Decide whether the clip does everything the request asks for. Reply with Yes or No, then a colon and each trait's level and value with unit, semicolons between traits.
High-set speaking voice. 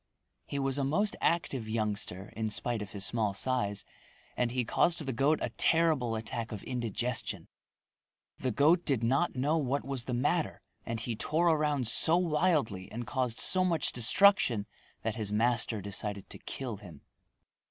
No: low, 125 Hz